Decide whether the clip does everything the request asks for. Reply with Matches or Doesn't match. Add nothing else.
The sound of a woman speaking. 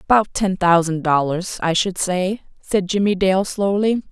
Matches